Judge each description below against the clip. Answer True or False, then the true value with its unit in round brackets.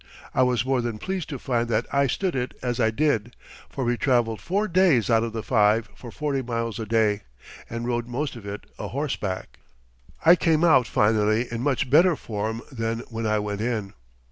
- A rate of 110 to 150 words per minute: False (200 wpm)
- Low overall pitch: True (120 Hz)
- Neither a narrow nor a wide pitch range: True (3.6 semitones)